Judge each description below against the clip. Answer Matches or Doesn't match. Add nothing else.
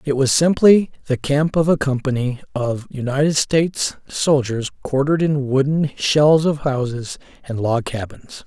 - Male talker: Matches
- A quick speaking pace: Doesn't match